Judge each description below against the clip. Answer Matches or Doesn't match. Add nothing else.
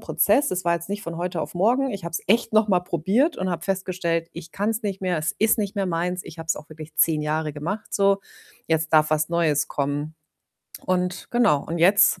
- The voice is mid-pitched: Matches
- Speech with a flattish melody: Doesn't match